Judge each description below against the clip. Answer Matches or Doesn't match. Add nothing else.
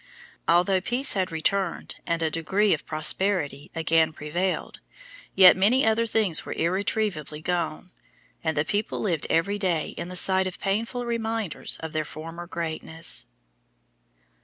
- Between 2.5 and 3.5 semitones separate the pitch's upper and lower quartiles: Doesn't match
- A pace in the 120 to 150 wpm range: Matches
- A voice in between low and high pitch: Matches